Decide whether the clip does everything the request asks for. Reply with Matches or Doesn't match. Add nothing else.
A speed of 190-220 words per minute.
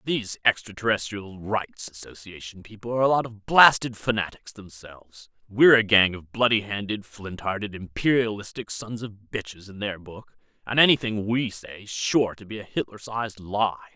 Doesn't match